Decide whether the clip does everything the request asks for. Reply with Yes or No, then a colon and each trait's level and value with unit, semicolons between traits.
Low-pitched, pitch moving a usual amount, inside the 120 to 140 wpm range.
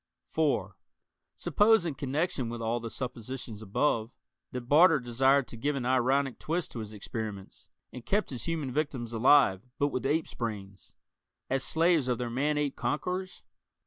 No: low, 130 Hz; average, 4.2 semitones; average, 160 wpm